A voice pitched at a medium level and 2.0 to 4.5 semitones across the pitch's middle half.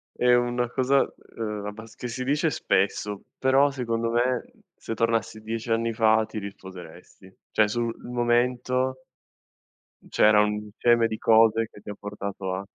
No: low, 115 Hz; narrow, 2.6 semitones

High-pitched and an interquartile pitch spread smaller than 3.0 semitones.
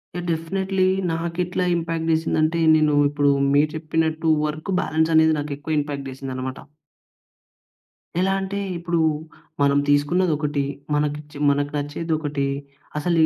No: medium, 155 Hz; narrow, 2.6 semitones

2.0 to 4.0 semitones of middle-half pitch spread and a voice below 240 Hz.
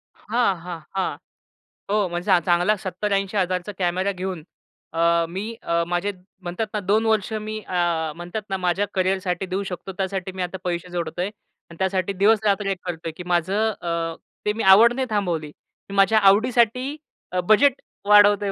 Yes: average, 2.9 semitones; high, 190 Hz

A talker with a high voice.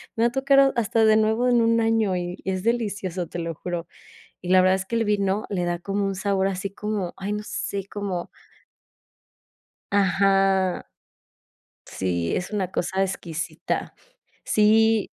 Yes: high, 195 Hz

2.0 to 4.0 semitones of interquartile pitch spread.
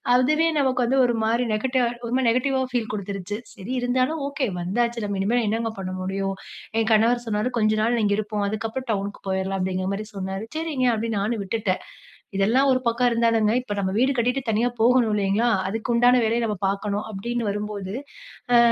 Yes: average, 3.3 semitones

